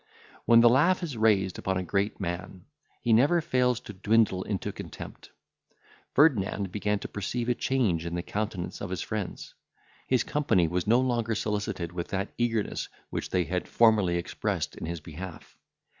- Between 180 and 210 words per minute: No, average, 170 wpm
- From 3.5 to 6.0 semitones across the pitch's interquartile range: Yes, average, 4.3 semitones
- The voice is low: Yes, low, 105 Hz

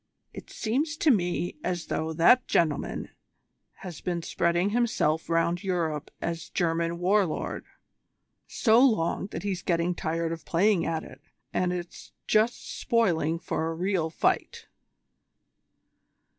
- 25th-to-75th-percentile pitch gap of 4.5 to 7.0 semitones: No, average, 3.6 semitones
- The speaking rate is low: Yes, slow, 130 wpm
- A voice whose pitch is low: No, medium, 175 Hz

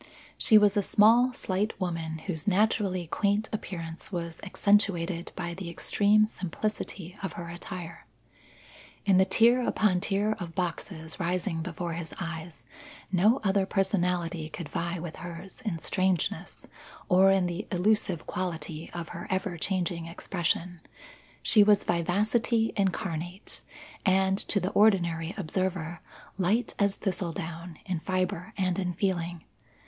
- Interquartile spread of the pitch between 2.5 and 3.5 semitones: Yes, average, 2.9 semitones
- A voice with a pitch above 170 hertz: Yes, medium, 185 Hz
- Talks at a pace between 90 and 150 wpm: Yes, slow, 135 wpm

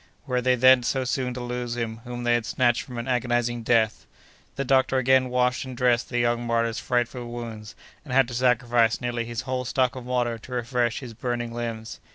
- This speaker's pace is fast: Yes, fast, 210 wpm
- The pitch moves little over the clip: Yes, narrow, 1.2 semitones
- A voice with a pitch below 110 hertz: No, low, 120 Hz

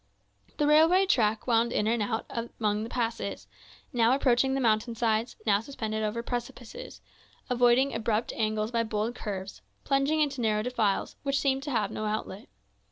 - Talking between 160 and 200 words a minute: Yes, average, 165 wpm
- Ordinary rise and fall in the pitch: Yes, average, 3.4 semitones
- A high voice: Yes, high, 230 Hz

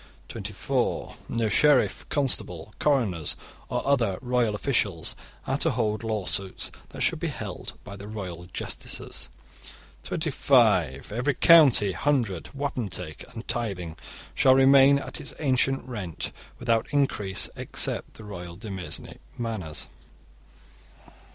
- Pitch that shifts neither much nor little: No, wide, 5.8 semitones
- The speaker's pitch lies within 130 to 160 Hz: No, low, 110 Hz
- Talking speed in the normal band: No, slow, 115 wpm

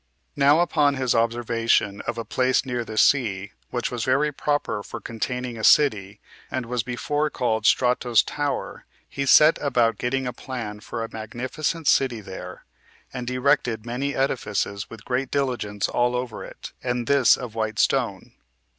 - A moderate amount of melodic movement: Yes, average, 3.0 semitones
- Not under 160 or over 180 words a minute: Yes, average, 165 wpm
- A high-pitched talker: No, low, 125 Hz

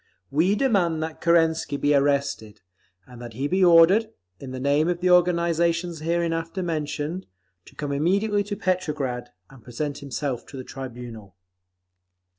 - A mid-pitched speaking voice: Yes, medium, 160 Hz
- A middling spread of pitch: Yes, average, 4.0 semitones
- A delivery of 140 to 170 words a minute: Yes, average, 145 wpm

